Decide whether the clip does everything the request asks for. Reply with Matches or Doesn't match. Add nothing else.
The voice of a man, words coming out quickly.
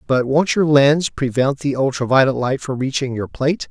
Matches